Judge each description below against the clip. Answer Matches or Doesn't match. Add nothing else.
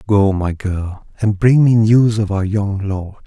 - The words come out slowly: Doesn't match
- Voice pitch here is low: Matches